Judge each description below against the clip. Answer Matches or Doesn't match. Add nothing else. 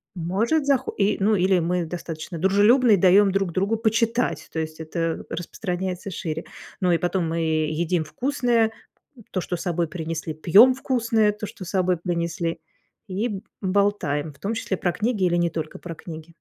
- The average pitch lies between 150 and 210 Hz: Matches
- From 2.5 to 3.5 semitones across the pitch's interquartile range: Doesn't match